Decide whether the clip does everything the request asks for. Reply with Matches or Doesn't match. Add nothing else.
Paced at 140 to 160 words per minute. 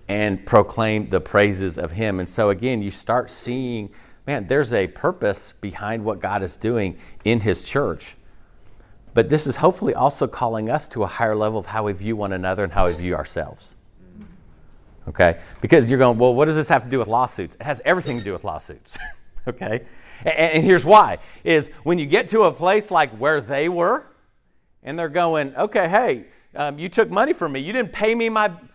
Doesn't match